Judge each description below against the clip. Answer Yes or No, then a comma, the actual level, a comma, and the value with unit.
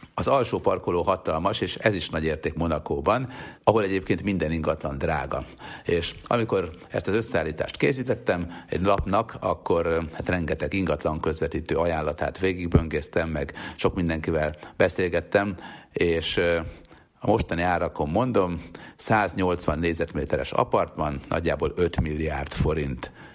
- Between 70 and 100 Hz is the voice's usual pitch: Yes, very low, 85 Hz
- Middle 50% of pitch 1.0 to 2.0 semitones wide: No, narrow, 2.4 semitones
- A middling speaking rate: Yes, average, 120 wpm